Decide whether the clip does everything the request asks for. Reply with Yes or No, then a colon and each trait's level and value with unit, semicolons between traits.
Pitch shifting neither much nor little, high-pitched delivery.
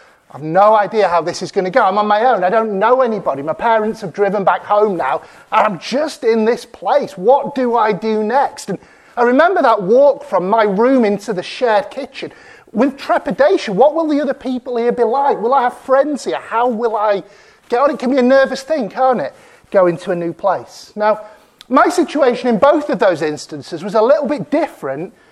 Yes: average, 5.0 semitones; high, 235 Hz